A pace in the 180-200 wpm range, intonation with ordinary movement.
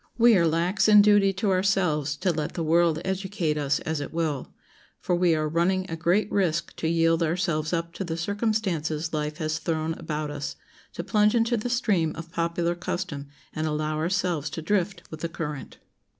Yes: average, 190 wpm; average, 3.5 semitones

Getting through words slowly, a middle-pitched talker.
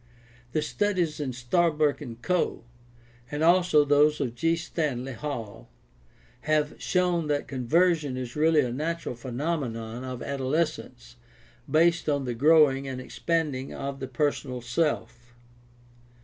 Yes: slow, 130 wpm; medium, 145 Hz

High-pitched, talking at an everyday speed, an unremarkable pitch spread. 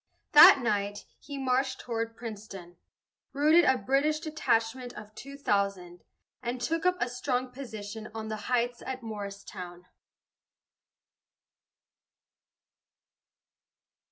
No: high, 235 Hz; slow, 100 wpm; average, 4.3 semitones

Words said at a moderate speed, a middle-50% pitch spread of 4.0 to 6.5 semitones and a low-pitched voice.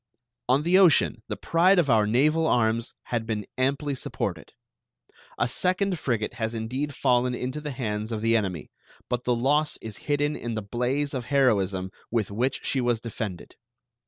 Yes: average, 170 wpm; average, 4.4 semitones; low, 125 Hz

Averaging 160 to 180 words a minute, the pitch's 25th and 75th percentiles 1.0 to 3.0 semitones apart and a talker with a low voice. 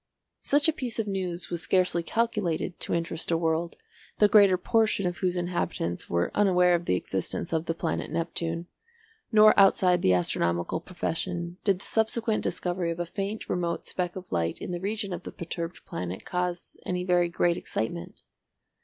No: average, 175 wpm; average, 2.7 semitones; medium, 175 Hz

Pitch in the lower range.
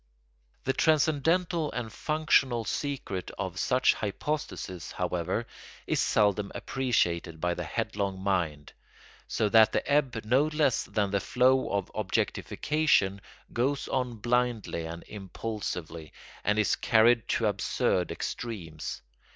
Yes: low, 110 Hz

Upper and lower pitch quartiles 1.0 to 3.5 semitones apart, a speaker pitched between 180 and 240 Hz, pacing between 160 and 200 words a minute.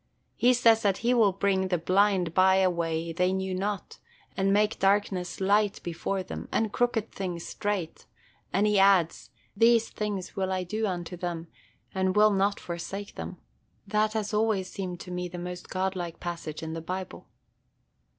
Yes: narrow, 2.5 semitones; high, 190 Hz; average, 170 wpm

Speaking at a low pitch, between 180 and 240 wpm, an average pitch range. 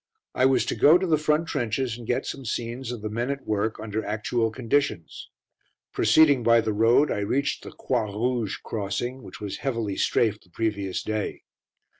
Yes: low, 115 Hz; average, 185 wpm; average, 3.7 semitones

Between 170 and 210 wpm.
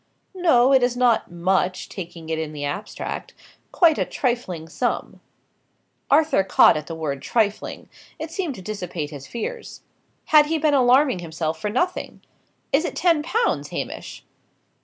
No: average, 155 wpm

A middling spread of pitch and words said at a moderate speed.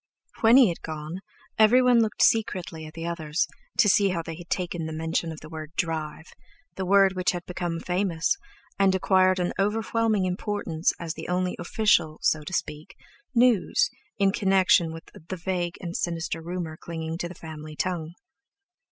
Yes: average, 3.2 semitones; average, 160 wpm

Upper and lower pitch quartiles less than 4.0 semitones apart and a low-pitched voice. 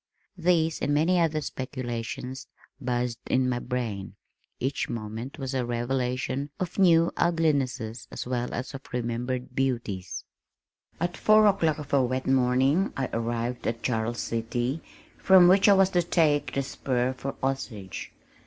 No: average, 4.3 semitones; low, 130 Hz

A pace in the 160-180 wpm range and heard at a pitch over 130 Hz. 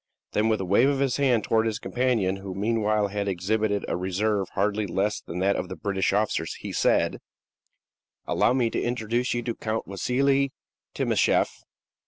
No: average, 175 wpm; low, 110 Hz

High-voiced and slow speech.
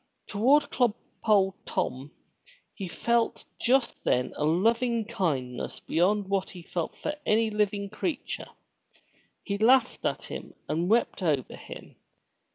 Yes: high, 205 Hz; slow, 125 wpm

